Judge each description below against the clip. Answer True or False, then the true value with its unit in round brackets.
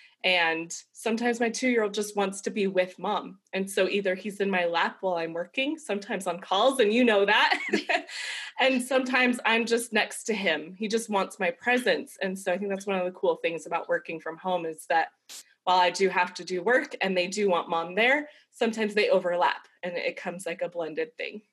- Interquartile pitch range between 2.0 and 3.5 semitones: False (4.4 semitones)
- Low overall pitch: False (200 Hz)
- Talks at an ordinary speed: False (225 wpm)